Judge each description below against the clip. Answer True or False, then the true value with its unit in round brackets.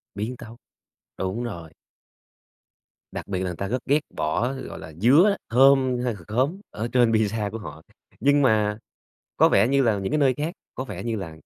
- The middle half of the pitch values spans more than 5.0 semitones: False (4.5 semitones)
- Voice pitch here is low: True (115 Hz)